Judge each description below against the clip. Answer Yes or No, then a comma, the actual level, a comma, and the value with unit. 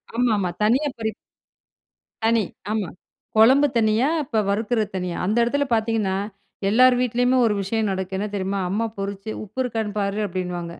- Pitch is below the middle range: No, high, 215 Hz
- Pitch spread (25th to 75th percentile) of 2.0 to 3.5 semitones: Yes, average, 2.9 semitones